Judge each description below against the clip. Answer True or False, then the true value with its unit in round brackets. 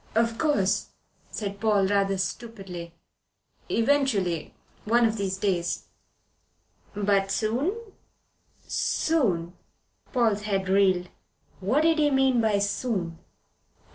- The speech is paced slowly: True (100 wpm)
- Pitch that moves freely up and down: False (4.0 semitones)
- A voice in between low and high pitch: False (205 Hz)